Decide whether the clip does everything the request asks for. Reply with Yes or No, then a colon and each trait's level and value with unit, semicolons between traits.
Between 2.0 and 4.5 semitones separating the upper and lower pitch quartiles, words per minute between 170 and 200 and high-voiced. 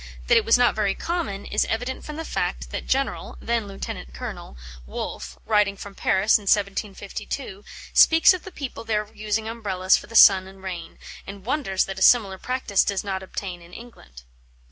Yes: average, 3.4 semitones; average, 185 wpm; high, 205 Hz